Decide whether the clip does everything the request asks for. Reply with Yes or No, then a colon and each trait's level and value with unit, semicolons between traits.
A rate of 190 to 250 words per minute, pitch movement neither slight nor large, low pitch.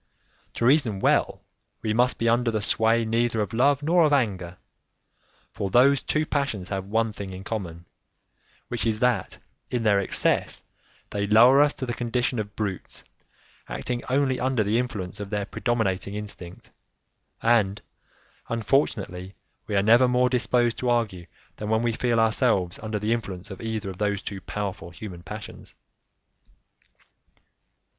No: average, 155 wpm; average, 3.4 semitones; low, 110 Hz